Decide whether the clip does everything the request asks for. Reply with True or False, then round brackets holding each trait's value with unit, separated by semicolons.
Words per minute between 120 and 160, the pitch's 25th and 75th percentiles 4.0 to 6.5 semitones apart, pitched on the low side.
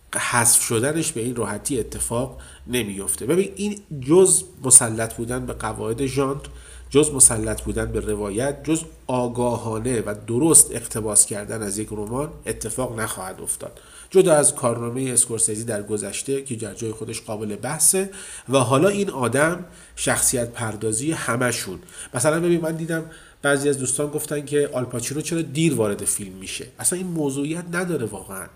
True (150 wpm; 5.4 semitones; 125 Hz)